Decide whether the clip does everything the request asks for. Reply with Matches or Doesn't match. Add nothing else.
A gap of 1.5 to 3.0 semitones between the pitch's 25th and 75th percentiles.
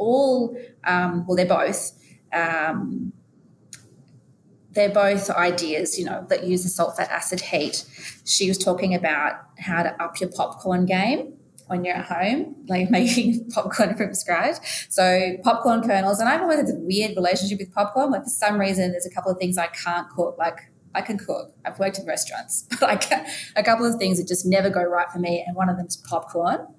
Doesn't match